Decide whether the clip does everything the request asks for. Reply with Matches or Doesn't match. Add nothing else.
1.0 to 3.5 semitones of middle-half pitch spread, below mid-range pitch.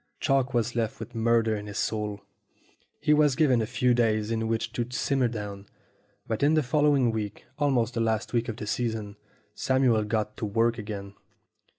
Matches